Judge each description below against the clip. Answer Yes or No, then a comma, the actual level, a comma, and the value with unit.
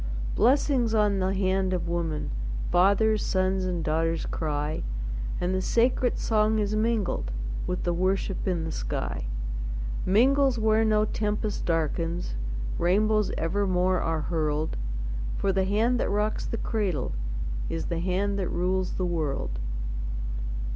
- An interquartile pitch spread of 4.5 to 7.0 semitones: No, average, 3.9 semitones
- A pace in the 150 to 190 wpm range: No, slow, 135 wpm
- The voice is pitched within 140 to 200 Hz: Yes, high, 190 Hz